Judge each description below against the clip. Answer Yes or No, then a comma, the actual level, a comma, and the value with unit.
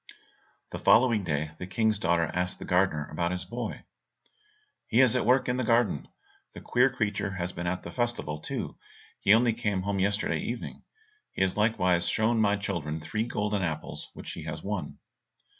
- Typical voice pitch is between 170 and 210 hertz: No, low, 100 Hz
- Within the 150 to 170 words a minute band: No, average, 180 wpm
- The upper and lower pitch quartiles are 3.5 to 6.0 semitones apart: Yes, average, 4.6 semitones